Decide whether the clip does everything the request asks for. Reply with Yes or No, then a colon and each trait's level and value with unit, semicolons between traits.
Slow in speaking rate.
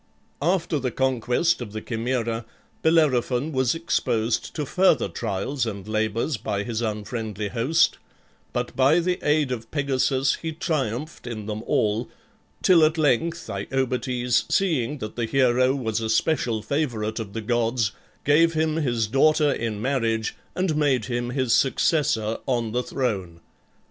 No: average, 145 wpm